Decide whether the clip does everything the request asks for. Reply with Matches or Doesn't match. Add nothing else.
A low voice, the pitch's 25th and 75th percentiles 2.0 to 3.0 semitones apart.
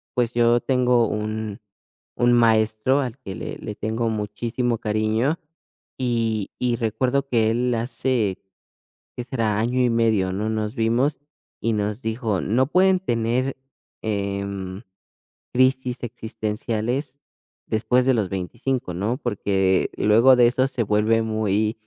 Matches